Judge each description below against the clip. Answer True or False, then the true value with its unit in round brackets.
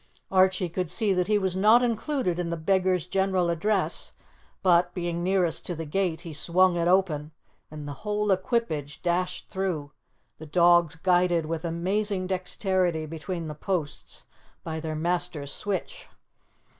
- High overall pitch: False (180 Hz)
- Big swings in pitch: False (2.6 semitones)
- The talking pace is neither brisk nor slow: True (150 wpm)